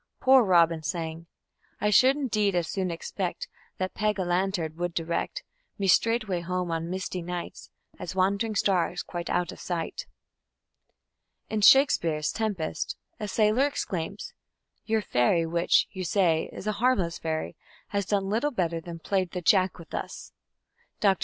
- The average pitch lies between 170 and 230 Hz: Yes, medium, 185 Hz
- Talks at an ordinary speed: Yes, average, 155 wpm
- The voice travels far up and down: No, average, 3.7 semitones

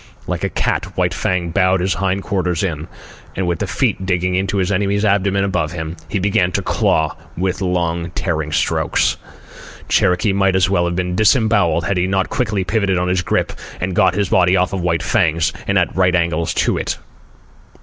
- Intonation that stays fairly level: Yes, narrow, 2.0 semitones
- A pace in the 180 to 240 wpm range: Yes, average, 190 wpm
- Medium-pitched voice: No, very low, 90 Hz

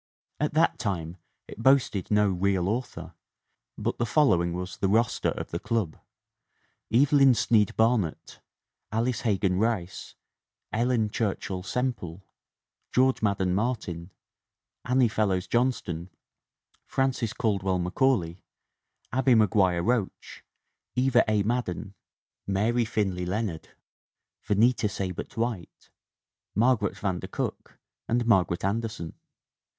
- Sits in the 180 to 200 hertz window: No, low, 105 Hz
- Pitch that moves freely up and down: No, average, 4.5 semitones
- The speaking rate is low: Yes, slow, 115 wpm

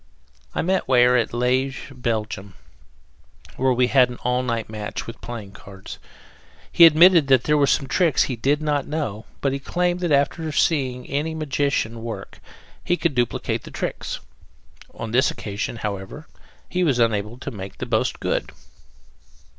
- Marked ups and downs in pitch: No, average, 4.4 semitones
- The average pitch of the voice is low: Yes, low, 130 Hz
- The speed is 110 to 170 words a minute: Yes, average, 165 wpm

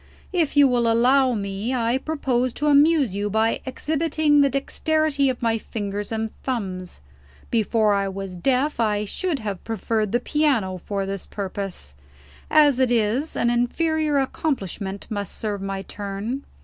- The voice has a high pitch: Yes, high, 230 Hz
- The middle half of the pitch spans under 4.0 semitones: No, wide, 5.6 semitones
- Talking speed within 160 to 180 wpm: No, average, 150 wpm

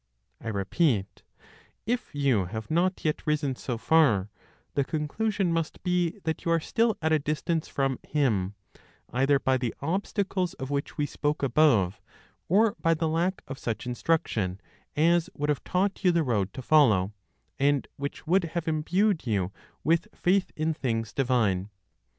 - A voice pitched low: No, medium, 150 Hz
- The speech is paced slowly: No, average, 160 wpm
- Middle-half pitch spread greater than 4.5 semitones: Yes, wide, 5.5 semitones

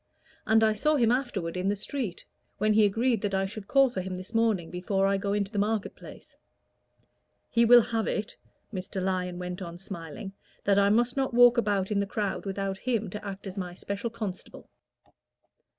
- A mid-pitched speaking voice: No, high, 200 Hz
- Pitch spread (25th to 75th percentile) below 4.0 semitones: Yes, average, 2.9 semitones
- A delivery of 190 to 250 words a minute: Yes, average, 200 wpm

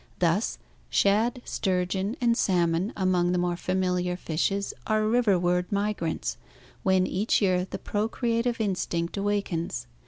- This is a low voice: No, high, 190 Hz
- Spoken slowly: Yes, slow, 120 wpm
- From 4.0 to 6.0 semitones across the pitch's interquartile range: No, average, 3.0 semitones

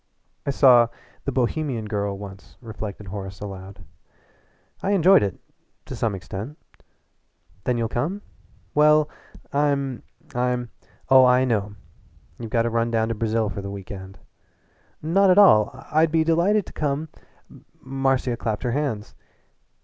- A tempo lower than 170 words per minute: Yes, average, 150 wpm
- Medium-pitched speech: No, low, 120 Hz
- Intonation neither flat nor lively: No, wide, 5.8 semitones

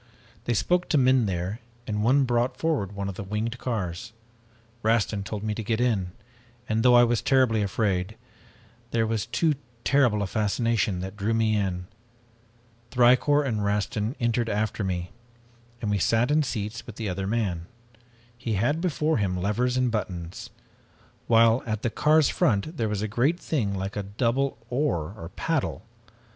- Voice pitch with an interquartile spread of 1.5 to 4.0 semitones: Yes, average, 3.5 semitones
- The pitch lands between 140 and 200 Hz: No, low, 110 Hz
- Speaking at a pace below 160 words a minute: No, average, 165 wpm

